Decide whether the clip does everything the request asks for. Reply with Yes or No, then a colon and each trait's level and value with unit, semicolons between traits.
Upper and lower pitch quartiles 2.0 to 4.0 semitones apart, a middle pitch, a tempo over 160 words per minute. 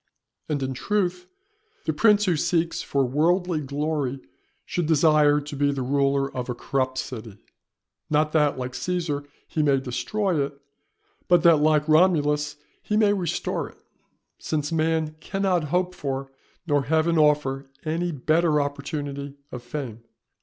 No: average, 3.2 semitones; medium, 150 Hz; average, 145 wpm